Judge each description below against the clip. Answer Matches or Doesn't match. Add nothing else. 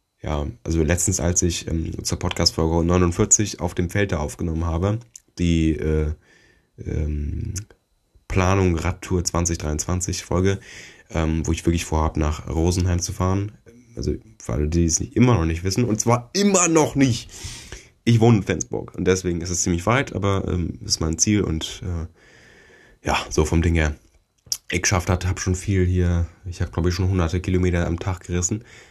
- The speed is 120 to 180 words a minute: Matches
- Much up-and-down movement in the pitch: Doesn't match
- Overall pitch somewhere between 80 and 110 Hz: Matches